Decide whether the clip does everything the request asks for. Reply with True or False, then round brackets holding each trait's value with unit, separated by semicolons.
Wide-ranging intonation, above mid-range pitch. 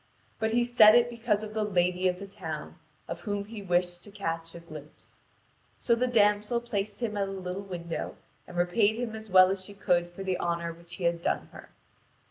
False (3.5 semitones; 195 Hz)